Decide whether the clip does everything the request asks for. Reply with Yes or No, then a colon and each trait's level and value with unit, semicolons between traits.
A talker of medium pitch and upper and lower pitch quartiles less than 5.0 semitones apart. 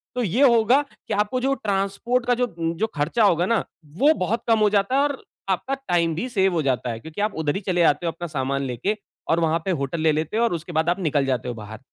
No: medium, 180 Hz; wide, 6.0 semitones